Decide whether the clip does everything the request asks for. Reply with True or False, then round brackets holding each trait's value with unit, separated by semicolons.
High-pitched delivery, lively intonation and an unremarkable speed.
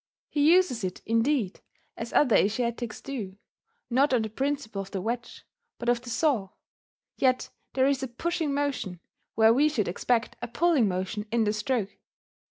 False (240 Hz; 4.4 semitones; 170 wpm)